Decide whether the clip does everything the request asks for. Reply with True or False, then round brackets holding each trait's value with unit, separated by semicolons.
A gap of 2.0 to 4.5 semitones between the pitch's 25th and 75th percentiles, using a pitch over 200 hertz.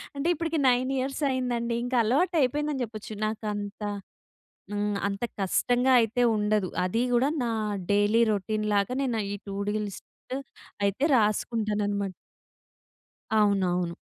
True (3.6 semitones; 220 Hz)